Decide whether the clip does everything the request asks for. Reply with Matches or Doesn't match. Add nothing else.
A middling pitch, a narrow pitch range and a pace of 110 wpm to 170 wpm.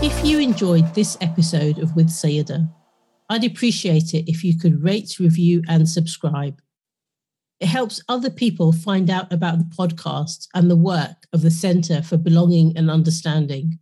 Matches